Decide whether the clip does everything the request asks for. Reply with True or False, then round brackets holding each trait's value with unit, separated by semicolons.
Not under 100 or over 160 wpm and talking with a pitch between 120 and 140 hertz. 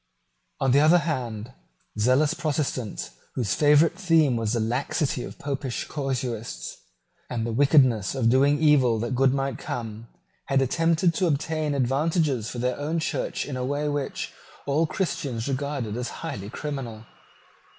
True (150 wpm; 135 Hz)